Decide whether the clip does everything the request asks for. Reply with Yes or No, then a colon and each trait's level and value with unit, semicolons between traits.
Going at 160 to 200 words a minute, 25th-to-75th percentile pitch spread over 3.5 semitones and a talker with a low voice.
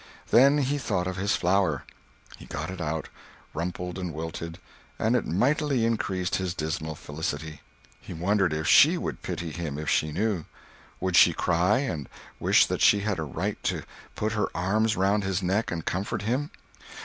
Yes: average, 175 wpm; average, 4.6 semitones; very low, 90 Hz